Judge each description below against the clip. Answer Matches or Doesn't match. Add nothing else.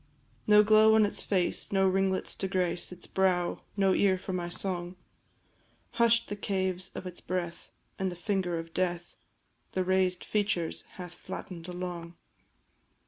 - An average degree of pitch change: Doesn't match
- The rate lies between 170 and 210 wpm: Doesn't match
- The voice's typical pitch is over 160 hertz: Matches